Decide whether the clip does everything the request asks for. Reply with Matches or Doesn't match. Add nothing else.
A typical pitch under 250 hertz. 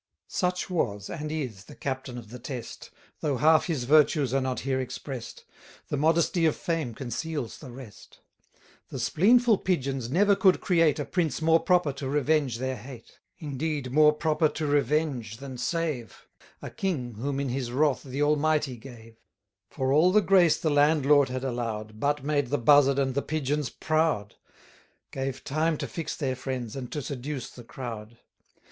Matches